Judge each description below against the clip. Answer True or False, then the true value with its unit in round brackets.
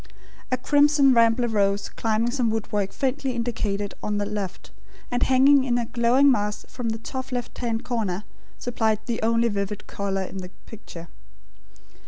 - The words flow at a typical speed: True (160 wpm)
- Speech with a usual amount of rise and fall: True (3.2 semitones)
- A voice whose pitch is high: True (230 Hz)